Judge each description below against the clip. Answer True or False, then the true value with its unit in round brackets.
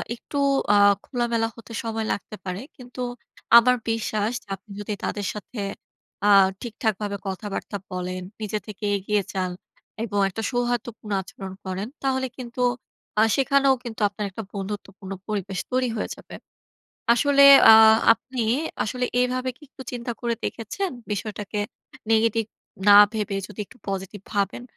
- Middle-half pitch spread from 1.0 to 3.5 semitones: True (3.2 semitones)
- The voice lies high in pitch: True (220 Hz)